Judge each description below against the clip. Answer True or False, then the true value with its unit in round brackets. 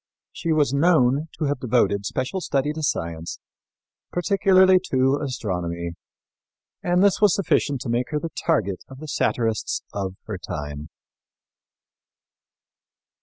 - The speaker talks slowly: True (125 wpm)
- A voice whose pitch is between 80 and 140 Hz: True (135 Hz)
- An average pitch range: False (8.3 semitones)